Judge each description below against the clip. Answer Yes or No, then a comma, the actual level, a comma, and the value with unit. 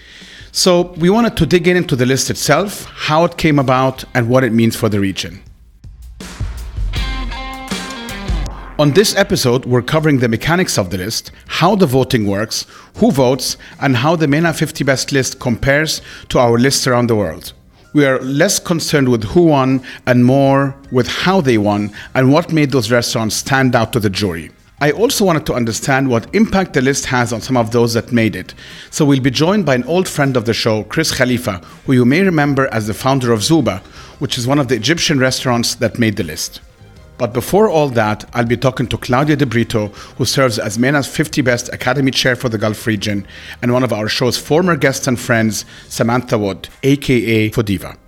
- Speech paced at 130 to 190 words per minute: No, average, 200 wpm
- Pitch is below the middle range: Yes, low, 125 Hz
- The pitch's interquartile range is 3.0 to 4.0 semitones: No, average, 4.5 semitones